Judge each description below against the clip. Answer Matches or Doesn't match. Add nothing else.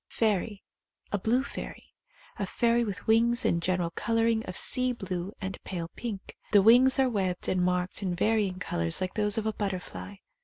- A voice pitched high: Matches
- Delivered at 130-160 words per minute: Doesn't match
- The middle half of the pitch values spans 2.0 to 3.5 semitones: Doesn't match